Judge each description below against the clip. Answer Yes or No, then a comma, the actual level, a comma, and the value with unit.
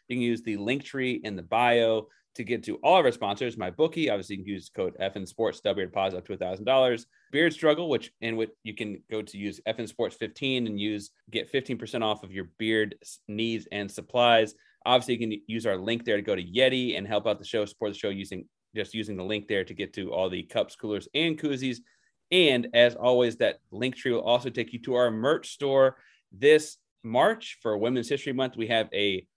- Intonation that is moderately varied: Yes, average, 3.4 semitones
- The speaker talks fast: Yes, fast, 235 wpm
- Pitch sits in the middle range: No, low, 115 Hz